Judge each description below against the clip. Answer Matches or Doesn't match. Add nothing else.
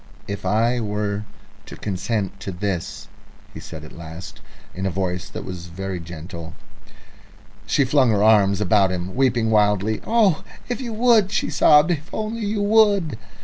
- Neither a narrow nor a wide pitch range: Doesn't match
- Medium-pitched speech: Doesn't match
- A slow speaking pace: Doesn't match